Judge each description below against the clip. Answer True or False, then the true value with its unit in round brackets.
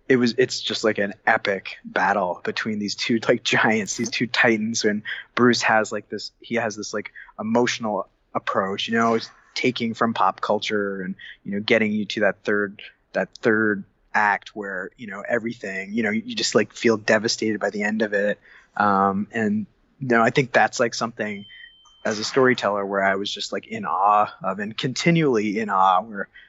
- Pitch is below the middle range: True (110 Hz)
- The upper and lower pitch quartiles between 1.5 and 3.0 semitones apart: True (2.5 semitones)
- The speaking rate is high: False (195 wpm)